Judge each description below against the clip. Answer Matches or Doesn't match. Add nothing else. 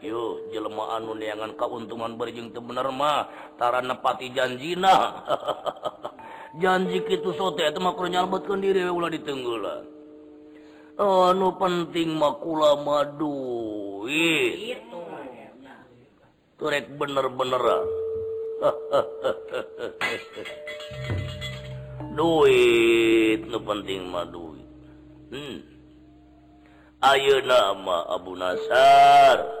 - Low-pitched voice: Doesn't match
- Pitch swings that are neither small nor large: Doesn't match